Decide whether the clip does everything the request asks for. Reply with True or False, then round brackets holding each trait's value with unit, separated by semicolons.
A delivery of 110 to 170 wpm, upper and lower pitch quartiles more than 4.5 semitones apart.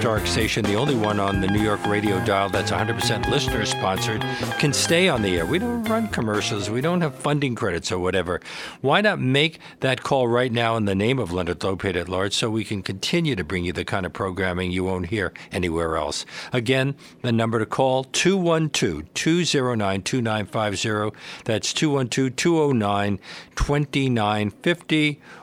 True (165 wpm; 5.6 semitones)